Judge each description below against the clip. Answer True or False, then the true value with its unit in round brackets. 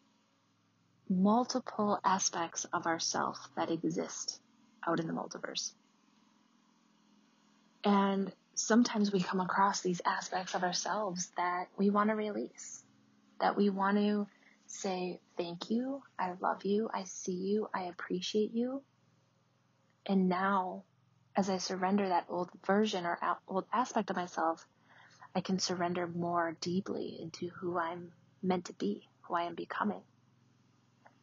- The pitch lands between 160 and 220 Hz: True (190 Hz)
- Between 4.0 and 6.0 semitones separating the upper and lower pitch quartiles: False (3.4 semitones)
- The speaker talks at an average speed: False (130 wpm)